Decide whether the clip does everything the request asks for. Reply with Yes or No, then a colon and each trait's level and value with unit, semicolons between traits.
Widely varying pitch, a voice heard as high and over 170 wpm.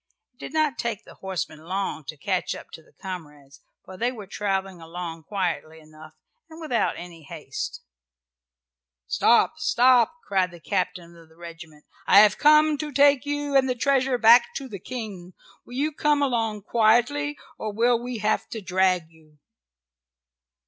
No: wide, 6.8 semitones; high, 210 Hz; average, 165 wpm